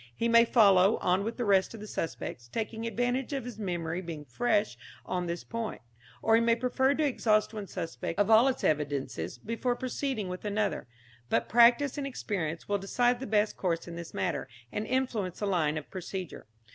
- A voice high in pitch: Yes, high, 210 Hz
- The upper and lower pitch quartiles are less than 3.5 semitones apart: No, average, 4.9 semitones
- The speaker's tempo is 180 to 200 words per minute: Yes, average, 195 wpm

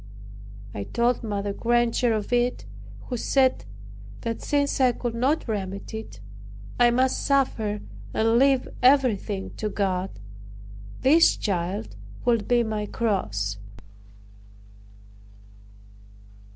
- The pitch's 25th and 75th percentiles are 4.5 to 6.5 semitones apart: No, average, 3.7 semitones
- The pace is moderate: No, slow, 105 wpm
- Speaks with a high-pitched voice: Yes, high, 230 Hz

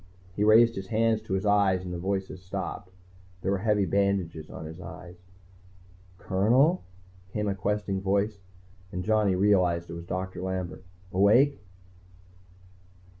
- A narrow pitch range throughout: Yes, narrow, 2.2 semitones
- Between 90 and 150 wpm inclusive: Yes, average, 140 wpm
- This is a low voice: Yes, very low, 95 Hz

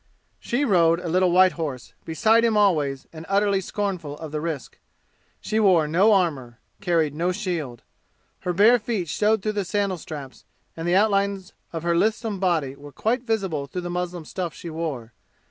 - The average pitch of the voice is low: No, medium, 180 Hz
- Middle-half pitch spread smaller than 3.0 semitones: No, average, 4.3 semitones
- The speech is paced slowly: No, average, 180 wpm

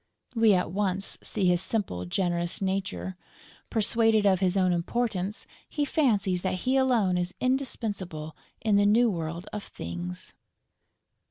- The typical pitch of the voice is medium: No, high, 195 Hz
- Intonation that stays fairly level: No, average, 3.9 semitones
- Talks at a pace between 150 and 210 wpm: No, average, 140 wpm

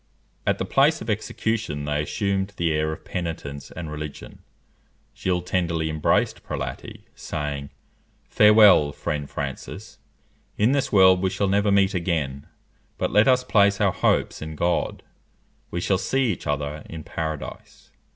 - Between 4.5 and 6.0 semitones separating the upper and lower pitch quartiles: Yes, average, 5.1 semitones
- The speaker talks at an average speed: Yes, average, 145 wpm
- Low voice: Yes, very low, 85 Hz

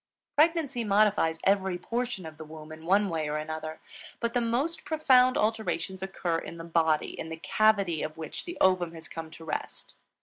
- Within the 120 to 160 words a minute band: No, average, 190 wpm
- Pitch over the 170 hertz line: Yes, medium, 185 Hz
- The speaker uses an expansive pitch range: Yes, wide, 6.1 semitones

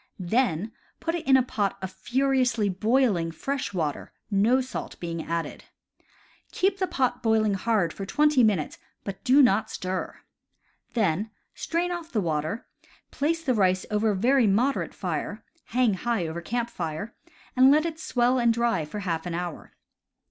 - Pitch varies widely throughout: Yes, wide, 5.9 semitones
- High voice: Yes, high, 225 Hz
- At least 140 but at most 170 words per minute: Yes, average, 165 wpm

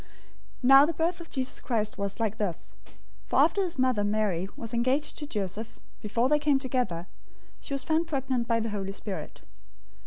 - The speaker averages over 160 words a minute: Yes, average, 185 wpm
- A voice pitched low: No, high, 240 Hz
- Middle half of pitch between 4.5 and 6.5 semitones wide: Yes, average, 5.0 semitones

